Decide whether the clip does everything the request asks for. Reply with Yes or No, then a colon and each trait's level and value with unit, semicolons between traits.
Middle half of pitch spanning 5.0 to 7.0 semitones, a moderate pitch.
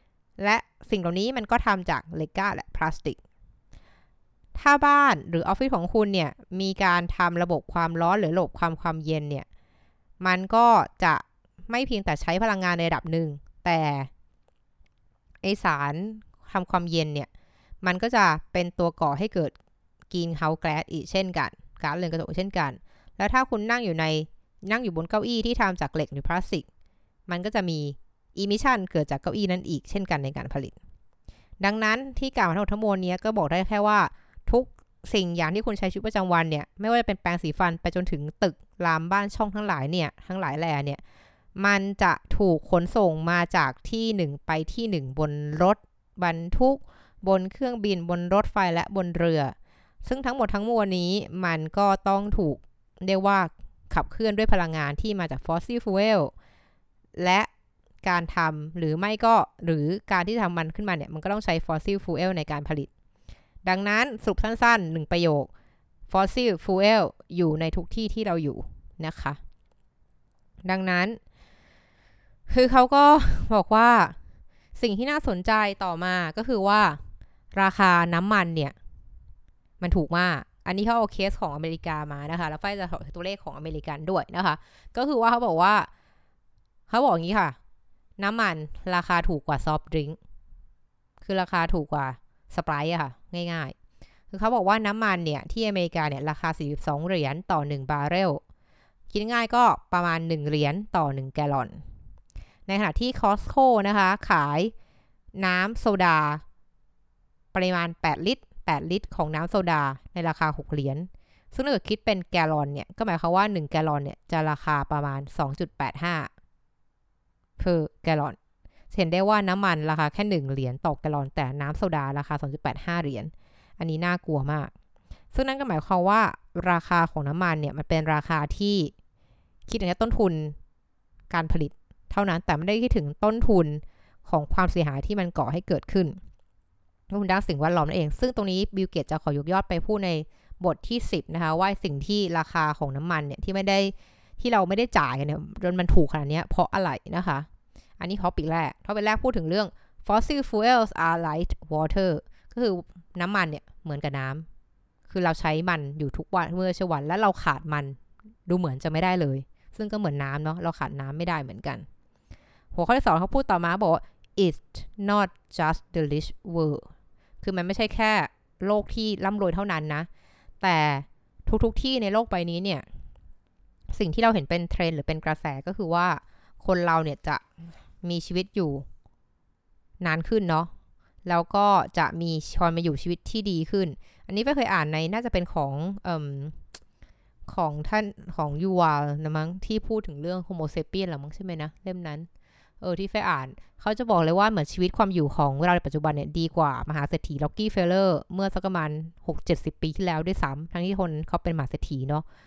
No: average, 4.5 semitones; medium, 175 Hz